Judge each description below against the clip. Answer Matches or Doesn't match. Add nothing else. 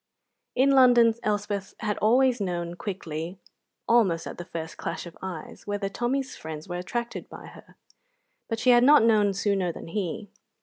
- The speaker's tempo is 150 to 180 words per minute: Matches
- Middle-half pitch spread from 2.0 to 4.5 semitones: Doesn't match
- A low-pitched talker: Doesn't match